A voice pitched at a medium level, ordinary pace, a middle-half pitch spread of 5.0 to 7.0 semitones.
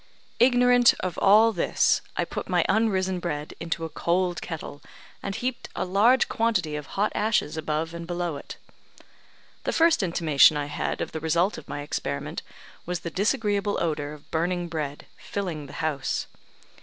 No: medium, 175 Hz; average, 165 wpm; average, 4.6 semitones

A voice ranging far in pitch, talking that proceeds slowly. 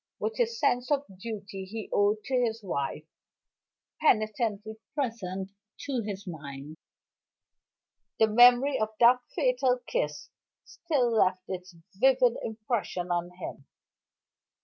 No: average, 4.9 semitones; slow, 120 wpm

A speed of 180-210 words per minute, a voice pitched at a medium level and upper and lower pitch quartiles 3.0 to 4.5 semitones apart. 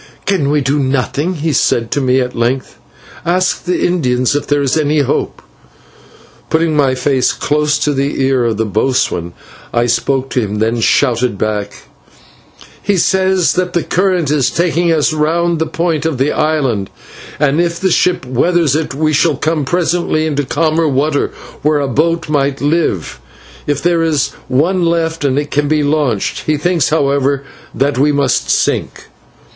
No: average, 170 wpm; medium, 145 Hz; average, 3.7 semitones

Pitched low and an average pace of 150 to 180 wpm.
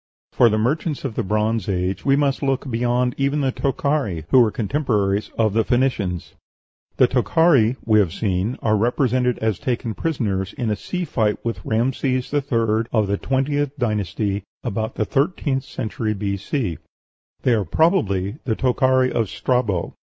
Yes: low, 115 Hz; average, 160 wpm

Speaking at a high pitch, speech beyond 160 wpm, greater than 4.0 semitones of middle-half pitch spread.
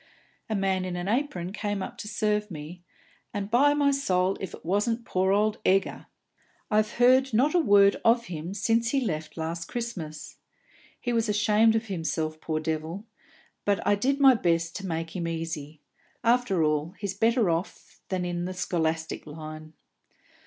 Yes: high, 195 Hz; average, 170 wpm; wide, 5.4 semitones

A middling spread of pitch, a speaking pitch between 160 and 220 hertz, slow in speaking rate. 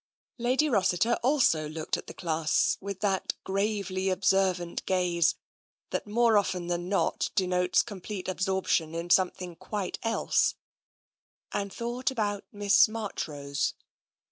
Yes: average, 3.0 semitones; high, 190 Hz; slow, 125 wpm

